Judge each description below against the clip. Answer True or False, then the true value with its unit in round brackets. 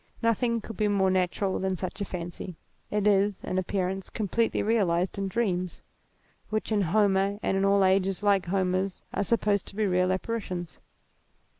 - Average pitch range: False (2.0 semitones)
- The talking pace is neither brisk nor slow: True (165 wpm)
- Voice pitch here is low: False (195 Hz)